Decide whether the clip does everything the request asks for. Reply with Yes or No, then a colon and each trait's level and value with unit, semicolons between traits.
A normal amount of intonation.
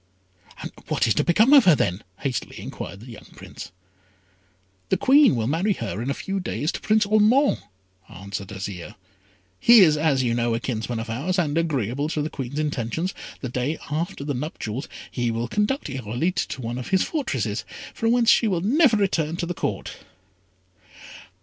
No: wide, 8.4 semitones